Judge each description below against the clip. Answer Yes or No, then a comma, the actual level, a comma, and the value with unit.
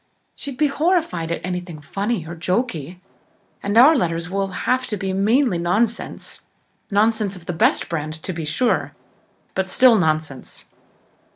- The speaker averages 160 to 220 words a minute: No, average, 150 wpm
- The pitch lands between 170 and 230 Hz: Yes, high, 190 Hz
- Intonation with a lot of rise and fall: Yes, wide, 5.7 semitones